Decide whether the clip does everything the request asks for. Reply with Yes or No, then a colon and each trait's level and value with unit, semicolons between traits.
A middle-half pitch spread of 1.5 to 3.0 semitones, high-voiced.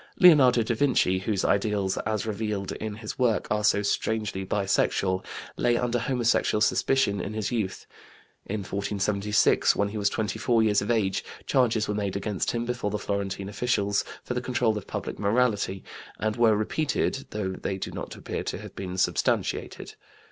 No: average, 2.7 semitones; low, 105 Hz